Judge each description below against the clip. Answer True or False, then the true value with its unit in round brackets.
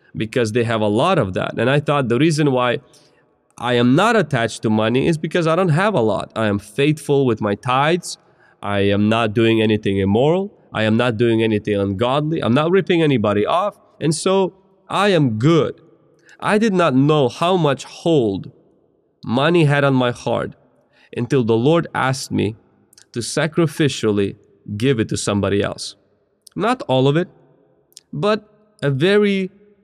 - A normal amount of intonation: False (6.7 semitones)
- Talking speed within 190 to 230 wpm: False (170 wpm)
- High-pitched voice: False (135 Hz)